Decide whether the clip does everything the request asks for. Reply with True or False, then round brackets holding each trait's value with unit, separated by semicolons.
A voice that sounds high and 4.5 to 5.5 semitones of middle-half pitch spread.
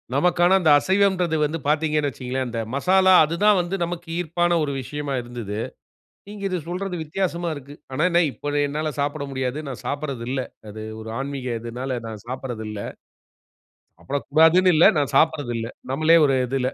False (145 Hz; 5.0 semitones)